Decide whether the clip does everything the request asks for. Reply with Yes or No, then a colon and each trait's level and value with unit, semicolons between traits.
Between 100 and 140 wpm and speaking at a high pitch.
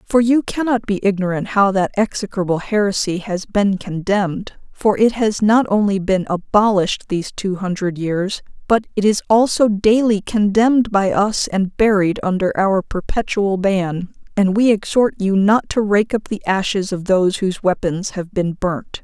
No: average, 170 wpm; high, 200 Hz